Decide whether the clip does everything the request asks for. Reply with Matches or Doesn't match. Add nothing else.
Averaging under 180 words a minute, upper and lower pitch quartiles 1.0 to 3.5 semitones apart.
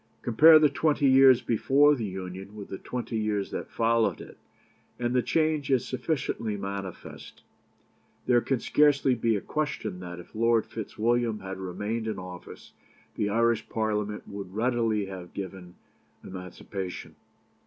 Doesn't match